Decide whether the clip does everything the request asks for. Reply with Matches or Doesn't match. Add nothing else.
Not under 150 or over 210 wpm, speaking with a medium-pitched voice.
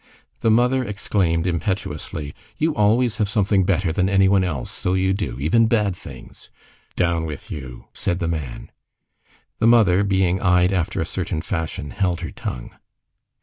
Doesn't match